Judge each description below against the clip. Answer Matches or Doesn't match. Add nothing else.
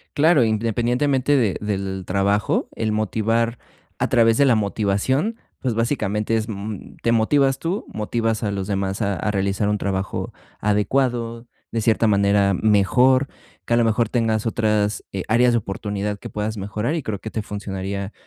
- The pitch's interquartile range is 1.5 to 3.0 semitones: Matches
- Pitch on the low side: Matches